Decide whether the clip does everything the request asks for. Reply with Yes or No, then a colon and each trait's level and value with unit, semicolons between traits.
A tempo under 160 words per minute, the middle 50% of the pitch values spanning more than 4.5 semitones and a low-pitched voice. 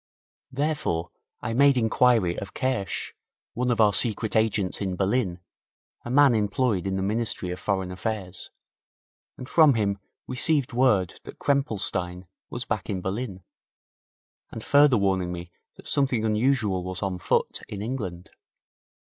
Yes: average, 140 wpm; average, 5.1 semitones; low, 105 Hz